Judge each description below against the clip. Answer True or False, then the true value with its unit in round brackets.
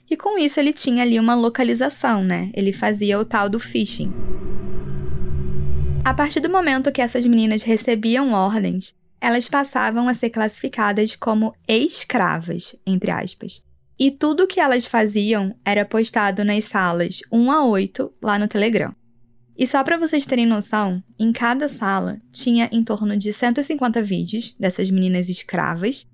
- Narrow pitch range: False (4.4 semitones)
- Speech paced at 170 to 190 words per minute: False (155 wpm)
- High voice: True (220 Hz)